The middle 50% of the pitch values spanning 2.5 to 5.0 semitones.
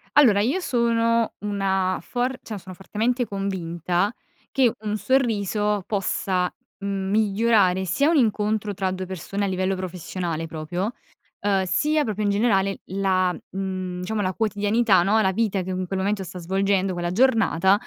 Yes: average, 2.8 semitones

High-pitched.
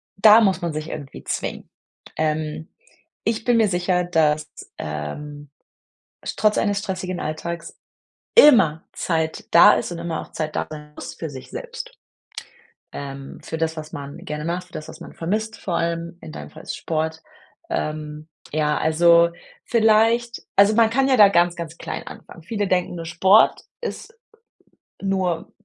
No: medium, 170 Hz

